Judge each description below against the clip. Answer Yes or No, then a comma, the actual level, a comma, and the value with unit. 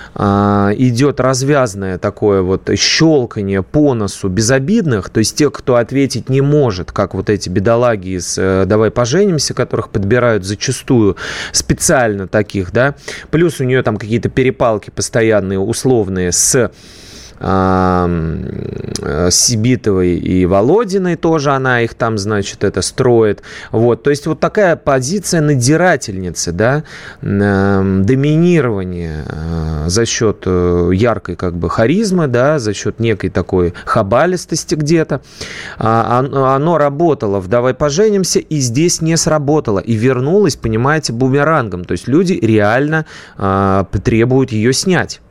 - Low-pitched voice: Yes, low, 115 Hz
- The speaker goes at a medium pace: Yes, average, 120 wpm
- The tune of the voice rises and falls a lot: Yes, wide, 6.6 semitones